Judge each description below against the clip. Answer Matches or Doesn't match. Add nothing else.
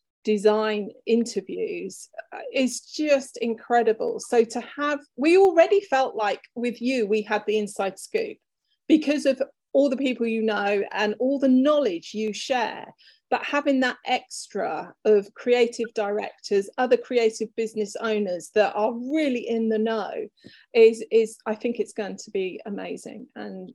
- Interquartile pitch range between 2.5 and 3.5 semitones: Doesn't match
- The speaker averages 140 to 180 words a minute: Matches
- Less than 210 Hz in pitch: Doesn't match